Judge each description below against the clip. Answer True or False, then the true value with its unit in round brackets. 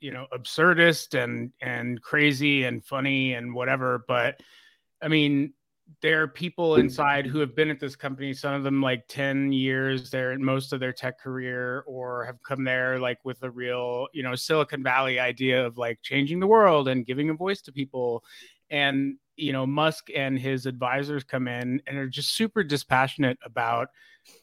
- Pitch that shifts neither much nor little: False (2.2 semitones)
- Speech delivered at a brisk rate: False (185 wpm)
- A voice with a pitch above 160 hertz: False (135 Hz)